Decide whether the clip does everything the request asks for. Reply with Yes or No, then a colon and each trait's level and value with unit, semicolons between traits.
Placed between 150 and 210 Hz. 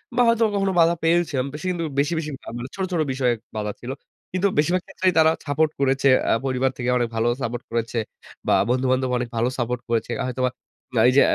No: low, 135 Hz